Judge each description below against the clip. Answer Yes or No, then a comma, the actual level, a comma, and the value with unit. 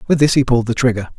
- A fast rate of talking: Yes, fast, 305 wpm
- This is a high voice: No, low, 125 Hz